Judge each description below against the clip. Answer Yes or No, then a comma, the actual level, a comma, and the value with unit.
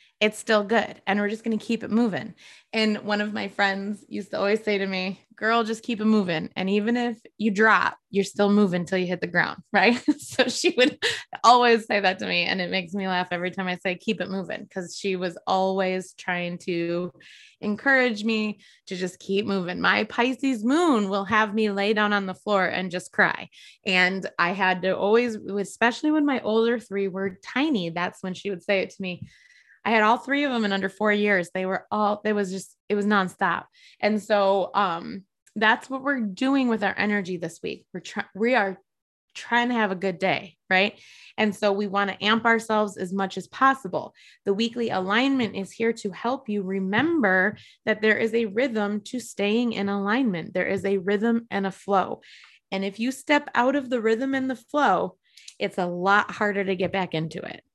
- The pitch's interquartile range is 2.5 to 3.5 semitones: Yes, average, 3.1 semitones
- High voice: Yes, high, 205 Hz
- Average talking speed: No, fast, 215 wpm